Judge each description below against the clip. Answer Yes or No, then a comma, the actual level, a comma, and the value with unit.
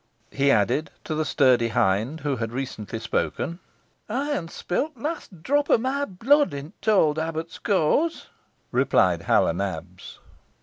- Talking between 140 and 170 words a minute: Yes, average, 150 wpm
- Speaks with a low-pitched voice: No, medium, 160 Hz